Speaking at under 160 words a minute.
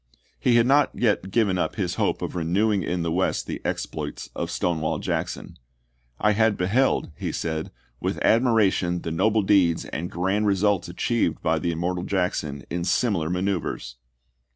No: average, 165 wpm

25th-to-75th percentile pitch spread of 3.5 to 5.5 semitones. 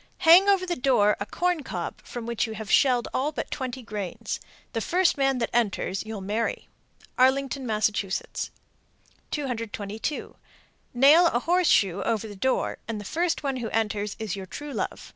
Yes: average, 5.0 semitones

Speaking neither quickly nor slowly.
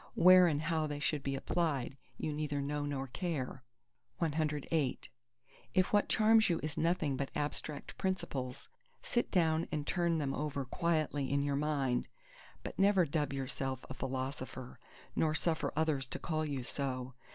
Yes: average, 155 wpm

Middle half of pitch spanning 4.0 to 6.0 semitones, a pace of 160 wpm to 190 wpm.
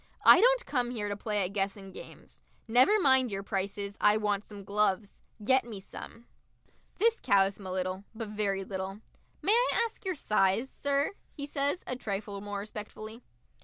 Yes: average, 4.7 semitones; average, 175 wpm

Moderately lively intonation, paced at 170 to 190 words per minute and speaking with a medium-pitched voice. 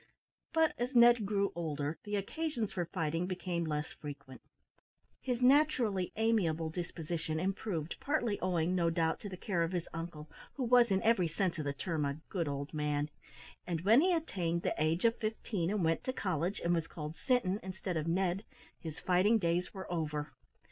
Yes: average, 4.8 semitones; average, 185 wpm; medium, 180 Hz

